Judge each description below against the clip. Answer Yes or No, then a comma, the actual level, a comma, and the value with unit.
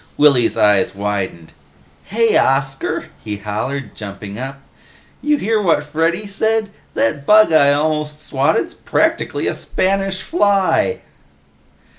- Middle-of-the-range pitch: Yes, medium, 150 Hz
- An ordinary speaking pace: No, slow, 115 wpm